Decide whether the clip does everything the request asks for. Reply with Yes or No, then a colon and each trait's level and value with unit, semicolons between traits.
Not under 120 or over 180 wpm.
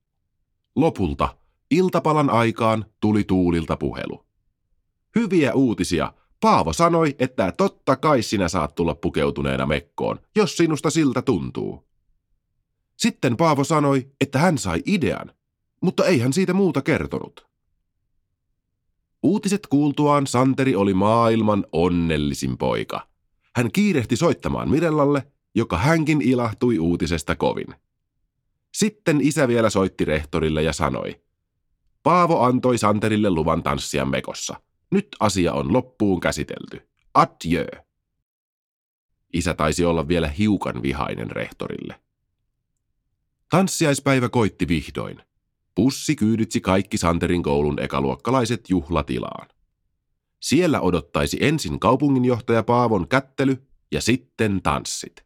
No: average, 105 wpm